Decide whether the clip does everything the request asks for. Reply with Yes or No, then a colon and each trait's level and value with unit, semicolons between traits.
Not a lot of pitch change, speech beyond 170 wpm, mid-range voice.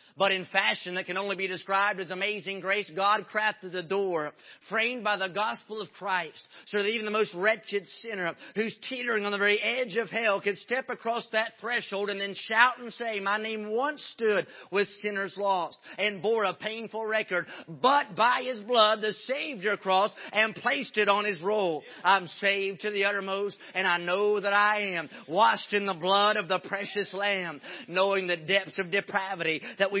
No: narrow, 2.1 semitones; average, 195 wpm; high, 200 Hz